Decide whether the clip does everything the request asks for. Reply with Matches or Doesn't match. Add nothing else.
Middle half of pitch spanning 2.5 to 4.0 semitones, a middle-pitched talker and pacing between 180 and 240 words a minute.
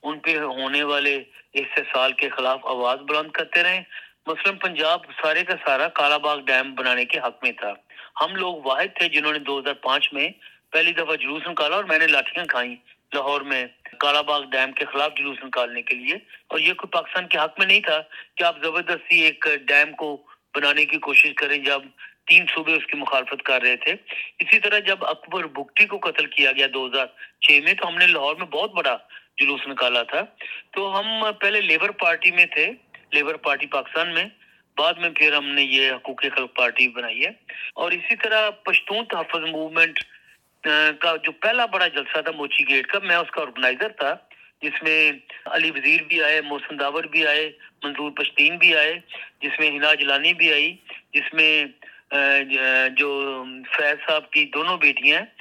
Matches